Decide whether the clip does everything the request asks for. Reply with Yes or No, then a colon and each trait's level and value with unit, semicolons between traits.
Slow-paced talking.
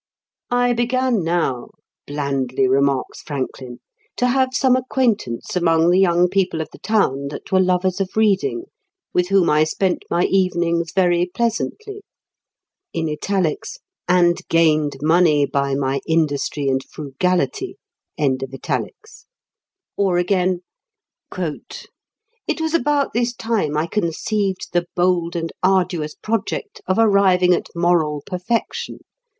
Yes: slow, 115 wpm